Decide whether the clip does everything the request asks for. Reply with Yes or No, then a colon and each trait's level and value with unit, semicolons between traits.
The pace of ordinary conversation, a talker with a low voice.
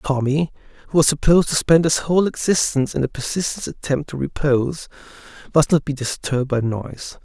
No: average, 175 wpm; medium, 145 Hz